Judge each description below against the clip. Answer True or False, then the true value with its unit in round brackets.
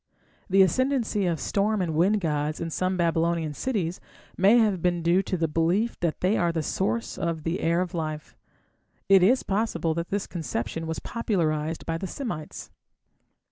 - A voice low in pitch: False (175 Hz)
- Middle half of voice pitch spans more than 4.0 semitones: False (3.3 semitones)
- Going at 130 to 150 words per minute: False (175 wpm)